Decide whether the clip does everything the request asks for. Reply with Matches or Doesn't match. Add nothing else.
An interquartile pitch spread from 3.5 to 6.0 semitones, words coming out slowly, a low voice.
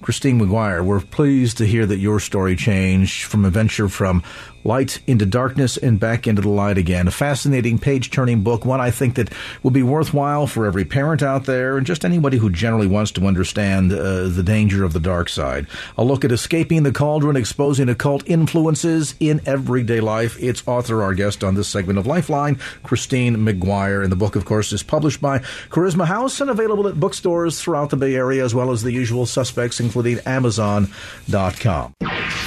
Doesn't match